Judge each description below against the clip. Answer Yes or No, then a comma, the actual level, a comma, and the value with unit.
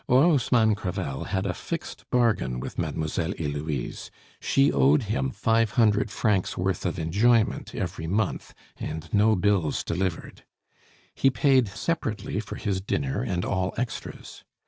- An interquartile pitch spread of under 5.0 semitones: No, wide, 5.6 semitones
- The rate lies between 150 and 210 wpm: No, slow, 135 wpm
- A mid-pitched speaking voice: No, low, 100 Hz